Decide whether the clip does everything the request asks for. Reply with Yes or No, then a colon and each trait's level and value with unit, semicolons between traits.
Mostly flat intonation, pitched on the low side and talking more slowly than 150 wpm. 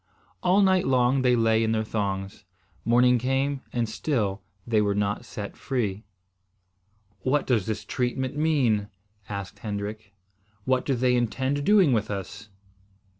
No: average, 4.0 semitones; low, 120 Hz; average, 140 wpm